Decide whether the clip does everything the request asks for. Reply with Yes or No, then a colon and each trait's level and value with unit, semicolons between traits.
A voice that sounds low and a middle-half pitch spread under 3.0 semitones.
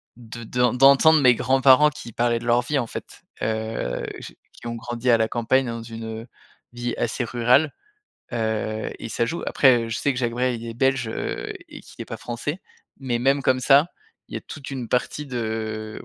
Yes: low, 120 Hz; narrow, 2.6 semitones